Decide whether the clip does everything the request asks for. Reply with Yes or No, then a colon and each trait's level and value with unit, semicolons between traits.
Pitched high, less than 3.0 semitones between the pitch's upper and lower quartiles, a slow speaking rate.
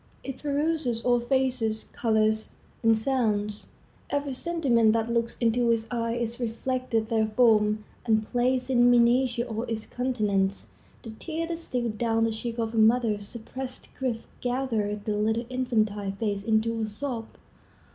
No: high, 230 Hz; narrow, 2.5 semitones; average, 145 wpm